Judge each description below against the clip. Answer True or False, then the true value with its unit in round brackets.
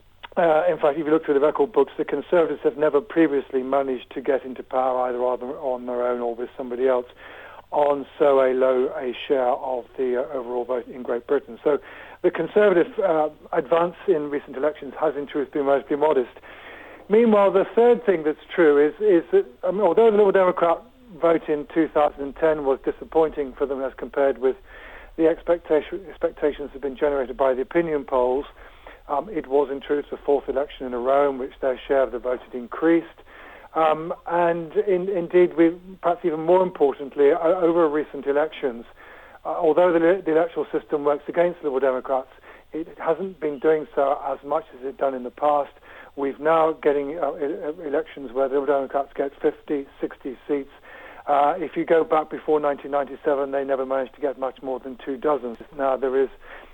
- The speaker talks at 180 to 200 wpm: True (190 wpm)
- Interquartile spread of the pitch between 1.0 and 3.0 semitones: False (3.4 semitones)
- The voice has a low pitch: False (145 Hz)